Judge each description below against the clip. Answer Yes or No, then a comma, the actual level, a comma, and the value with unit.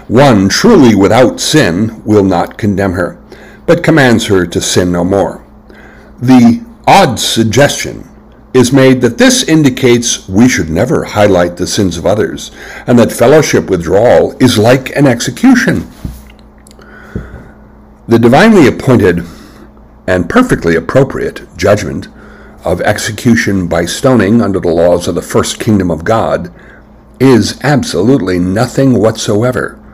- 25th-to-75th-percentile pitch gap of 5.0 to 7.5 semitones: Yes, average, 5.3 semitones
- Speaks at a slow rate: Yes, slow, 125 wpm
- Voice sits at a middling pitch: No, low, 115 Hz